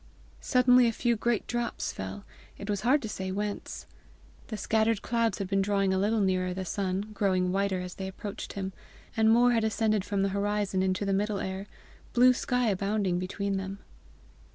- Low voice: No, high, 200 Hz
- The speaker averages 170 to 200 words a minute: Yes, average, 185 wpm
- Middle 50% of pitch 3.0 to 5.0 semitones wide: No, narrow, 2.6 semitones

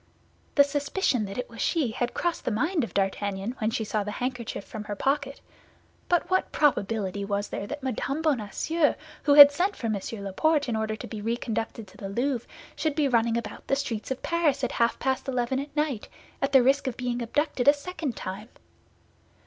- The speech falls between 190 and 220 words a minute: Yes, average, 200 wpm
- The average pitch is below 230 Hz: No, very high, 250 Hz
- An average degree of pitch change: Yes, average, 4.8 semitones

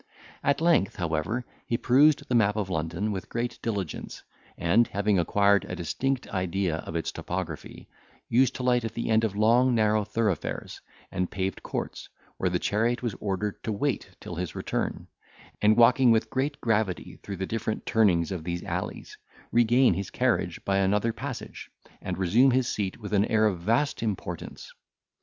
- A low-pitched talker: Yes, low, 105 Hz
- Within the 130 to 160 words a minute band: No, average, 170 wpm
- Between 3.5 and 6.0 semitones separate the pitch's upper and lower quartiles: Yes, average, 4.1 semitones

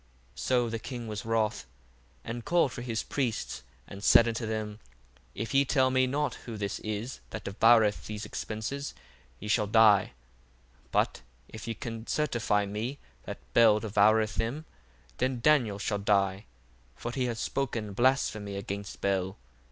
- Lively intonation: No, average, 2.8 semitones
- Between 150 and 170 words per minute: Yes, average, 160 wpm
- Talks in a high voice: No, low, 110 Hz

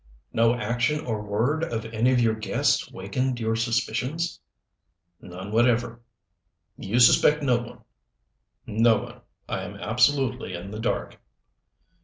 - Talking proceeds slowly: Yes, slow, 130 wpm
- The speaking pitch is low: Yes, low, 115 Hz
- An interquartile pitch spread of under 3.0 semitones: Yes, narrow, 2.4 semitones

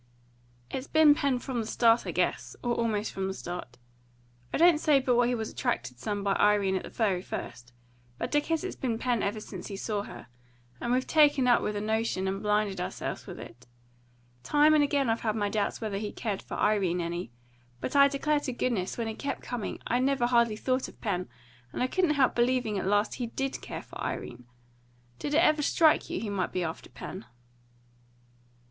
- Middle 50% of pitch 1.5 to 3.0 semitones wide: No, average, 4.8 semitones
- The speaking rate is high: Yes, fast, 210 wpm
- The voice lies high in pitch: Yes, high, 225 Hz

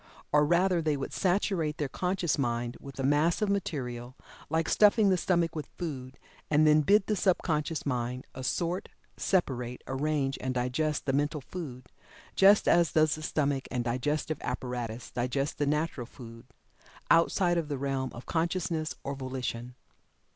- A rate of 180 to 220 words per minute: No, average, 155 wpm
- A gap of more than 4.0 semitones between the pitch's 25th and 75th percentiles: Yes, average, 4.7 semitones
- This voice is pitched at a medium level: Yes, medium, 150 Hz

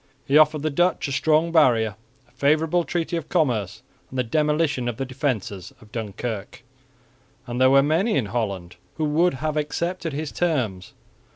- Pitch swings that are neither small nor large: Yes, average, 4.9 semitones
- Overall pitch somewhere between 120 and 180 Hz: Yes, medium, 140 Hz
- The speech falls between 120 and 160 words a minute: No, average, 170 wpm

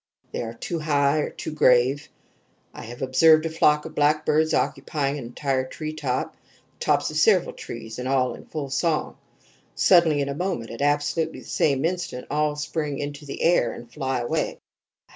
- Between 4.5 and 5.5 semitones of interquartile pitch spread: No, average, 2.9 semitones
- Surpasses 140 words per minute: Yes, average, 180 wpm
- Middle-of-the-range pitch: Yes, medium, 145 Hz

